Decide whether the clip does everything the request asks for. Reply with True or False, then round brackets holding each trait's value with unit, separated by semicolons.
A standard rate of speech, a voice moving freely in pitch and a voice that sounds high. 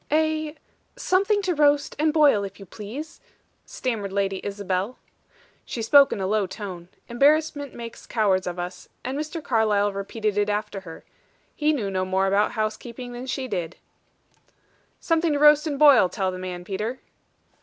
True (165 wpm; 6.9 semitones; 220 Hz)